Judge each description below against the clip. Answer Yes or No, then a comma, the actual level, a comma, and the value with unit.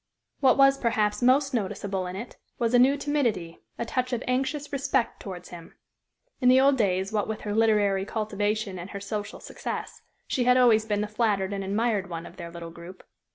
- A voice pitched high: Yes, high, 215 Hz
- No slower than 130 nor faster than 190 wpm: No, average, 200 wpm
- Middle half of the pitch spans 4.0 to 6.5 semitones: Yes, average, 4.3 semitones